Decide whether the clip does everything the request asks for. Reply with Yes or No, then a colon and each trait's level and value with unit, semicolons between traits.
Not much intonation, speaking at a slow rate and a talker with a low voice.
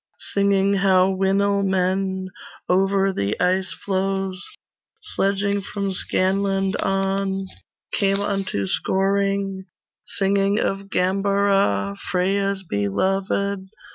No: narrow, 0.9 semitones; slow, 80 wpm; high, 195 Hz